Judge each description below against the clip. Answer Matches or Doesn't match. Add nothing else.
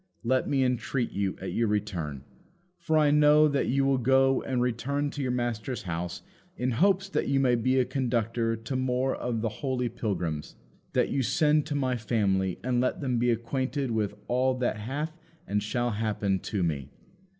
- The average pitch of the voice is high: Doesn't match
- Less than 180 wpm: Doesn't match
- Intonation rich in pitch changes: Doesn't match